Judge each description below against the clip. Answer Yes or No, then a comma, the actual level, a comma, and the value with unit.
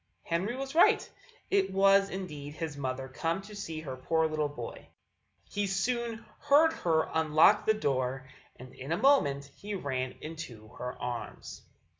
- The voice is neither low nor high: Yes, medium, 160 Hz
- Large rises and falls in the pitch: Yes, wide, 7.1 semitones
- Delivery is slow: No, average, 155 wpm